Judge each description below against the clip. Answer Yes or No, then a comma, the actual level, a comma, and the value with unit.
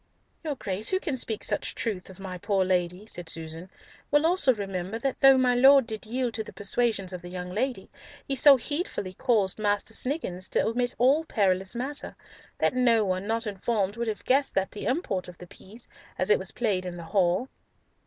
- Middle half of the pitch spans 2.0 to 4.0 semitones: No, average, 5.3 semitones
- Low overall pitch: No, high, 215 Hz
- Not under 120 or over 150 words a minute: No, fast, 205 wpm